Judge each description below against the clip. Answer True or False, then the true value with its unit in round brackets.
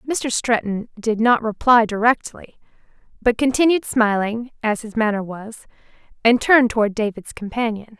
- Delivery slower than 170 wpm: True (135 wpm)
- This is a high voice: True (225 Hz)